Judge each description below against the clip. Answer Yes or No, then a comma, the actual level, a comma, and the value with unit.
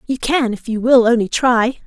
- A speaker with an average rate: No, fast, 225 wpm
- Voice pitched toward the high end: Yes, high, 240 Hz